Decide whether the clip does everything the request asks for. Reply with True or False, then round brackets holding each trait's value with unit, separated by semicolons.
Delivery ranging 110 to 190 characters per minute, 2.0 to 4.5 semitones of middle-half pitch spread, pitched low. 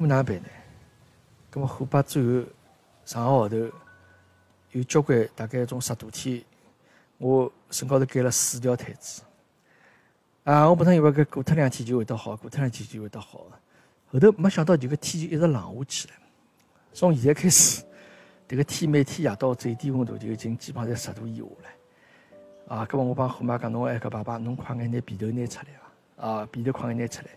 False (285 characters per minute; 3.7 semitones; 125 Hz)